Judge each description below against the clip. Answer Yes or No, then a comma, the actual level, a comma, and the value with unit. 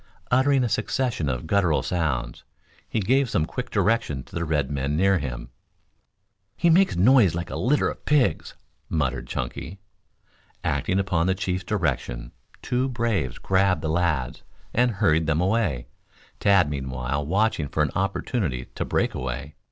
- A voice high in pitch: No, very low, 90 Hz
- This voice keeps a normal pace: Yes, average, 155 wpm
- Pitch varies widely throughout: Yes, wide, 7.5 semitones